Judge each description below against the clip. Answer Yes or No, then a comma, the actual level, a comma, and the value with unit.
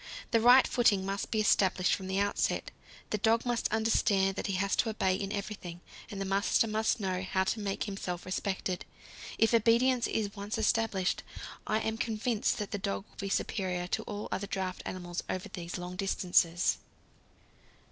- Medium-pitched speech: No, high, 200 Hz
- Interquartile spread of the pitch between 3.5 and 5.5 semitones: No, average, 2.8 semitones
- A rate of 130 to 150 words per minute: No, average, 180 wpm